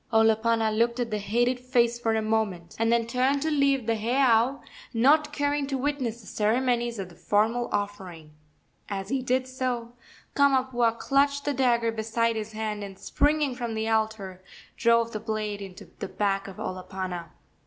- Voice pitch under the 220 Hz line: No, high, 230 Hz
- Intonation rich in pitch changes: No, average, 3.2 semitones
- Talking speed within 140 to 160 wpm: No, average, 170 wpm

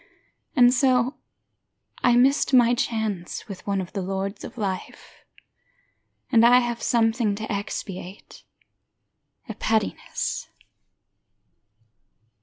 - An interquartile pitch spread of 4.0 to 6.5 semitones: No, average, 3.5 semitones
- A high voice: Yes, high, 225 Hz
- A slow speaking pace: Yes, slow, 100 wpm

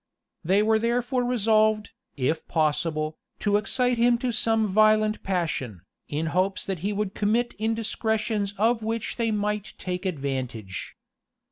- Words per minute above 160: No, slow, 135 wpm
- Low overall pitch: No, high, 210 Hz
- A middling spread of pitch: Yes, average, 4.0 semitones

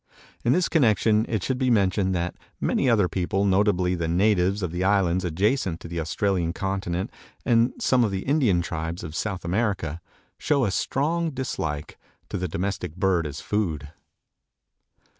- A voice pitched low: Yes, very low, 95 Hz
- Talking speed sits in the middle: Yes, average, 165 wpm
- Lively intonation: No, average, 4.0 semitones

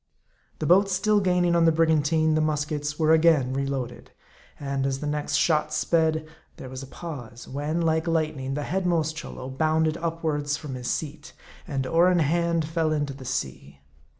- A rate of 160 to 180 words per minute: Yes, average, 175 wpm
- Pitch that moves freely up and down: No, average, 2.7 semitones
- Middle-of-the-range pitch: Yes, medium, 155 Hz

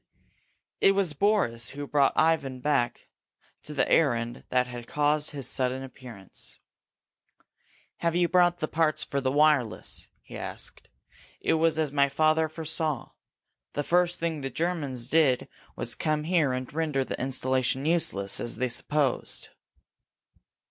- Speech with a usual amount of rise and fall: Yes, average, 3.9 semitones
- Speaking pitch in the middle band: Yes, medium, 145 Hz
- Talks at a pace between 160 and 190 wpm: No, average, 145 wpm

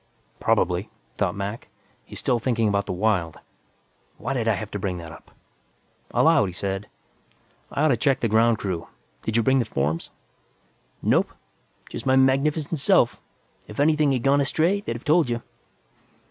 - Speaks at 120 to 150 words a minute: No, average, 170 wpm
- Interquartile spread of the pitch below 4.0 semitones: No, average, 5.3 semitones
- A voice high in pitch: No, low, 115 Hz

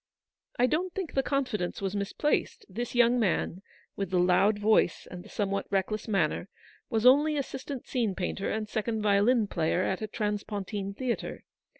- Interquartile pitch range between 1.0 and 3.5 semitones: No, average, 4.0 semitones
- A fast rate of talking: No, average, 185 wpm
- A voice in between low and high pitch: No, high, 210 Hz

